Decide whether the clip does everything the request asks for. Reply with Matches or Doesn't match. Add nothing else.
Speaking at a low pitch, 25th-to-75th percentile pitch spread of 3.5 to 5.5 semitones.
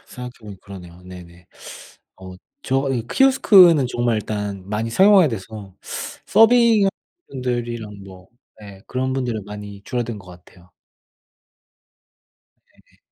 Matches